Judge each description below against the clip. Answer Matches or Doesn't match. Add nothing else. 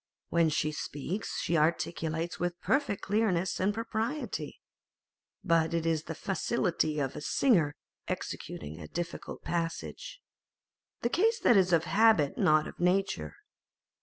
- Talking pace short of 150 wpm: Matches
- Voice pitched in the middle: Matches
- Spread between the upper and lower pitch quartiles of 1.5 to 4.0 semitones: Doesn't match